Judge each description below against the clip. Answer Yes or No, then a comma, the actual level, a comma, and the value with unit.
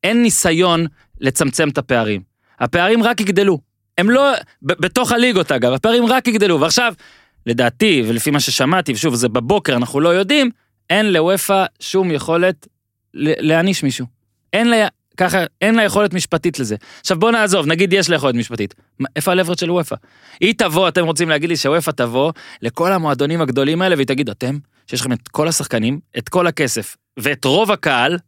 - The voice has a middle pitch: Yes, medium, 165 Hz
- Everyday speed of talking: No, fast, 170 wpm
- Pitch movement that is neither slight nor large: No, wide, 6.3 semitones